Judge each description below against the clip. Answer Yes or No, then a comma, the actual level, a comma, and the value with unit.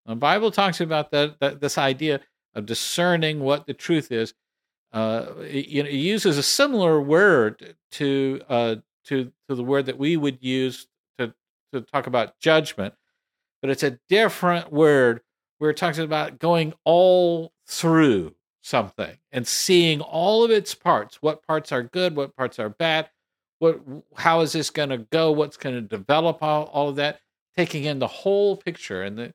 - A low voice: No, medium, 150 Hz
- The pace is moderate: Yes, average, 175 wpm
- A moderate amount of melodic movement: Yes, average, 3.6 semitones